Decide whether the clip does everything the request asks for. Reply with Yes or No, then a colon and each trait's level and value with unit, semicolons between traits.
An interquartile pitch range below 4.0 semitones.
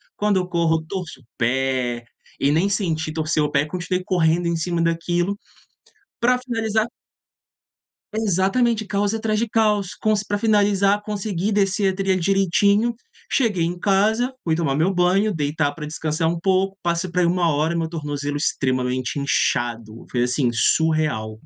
No: average, 4.8 semitones